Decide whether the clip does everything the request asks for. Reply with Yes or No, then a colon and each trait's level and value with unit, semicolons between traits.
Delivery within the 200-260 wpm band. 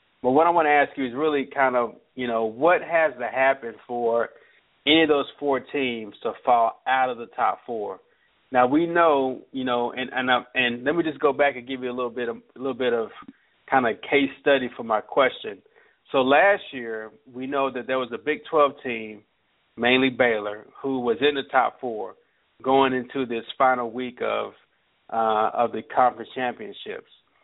Yes: fast, 205 wpm